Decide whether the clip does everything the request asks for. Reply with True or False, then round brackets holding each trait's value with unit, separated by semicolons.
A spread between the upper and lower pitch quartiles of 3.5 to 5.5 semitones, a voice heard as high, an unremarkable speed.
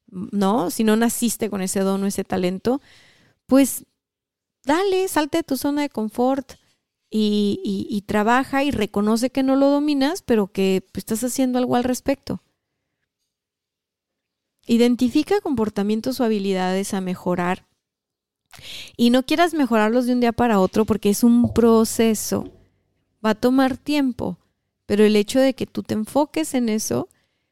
True (4.6 semitones; 235 Hz; 150 wpm)